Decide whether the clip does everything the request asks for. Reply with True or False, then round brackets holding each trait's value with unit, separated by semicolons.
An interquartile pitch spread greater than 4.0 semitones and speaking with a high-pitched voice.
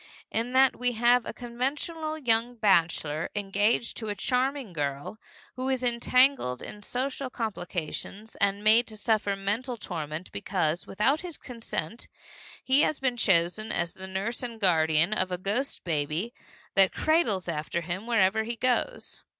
True (5.1 semitones; 220 Hz)